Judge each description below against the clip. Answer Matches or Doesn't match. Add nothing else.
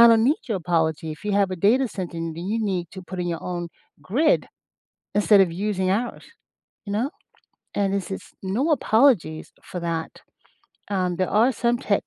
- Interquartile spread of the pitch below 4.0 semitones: Doesn't match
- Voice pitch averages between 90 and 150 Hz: Doesn't match